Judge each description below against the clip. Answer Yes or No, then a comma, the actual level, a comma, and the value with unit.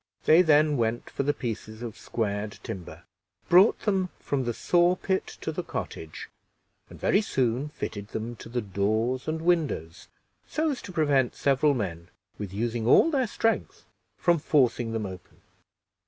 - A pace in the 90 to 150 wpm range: No, average, 160 wpm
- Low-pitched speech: Yes, low, 125 Hz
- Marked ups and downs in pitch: Yes, wide, 6.9 semitones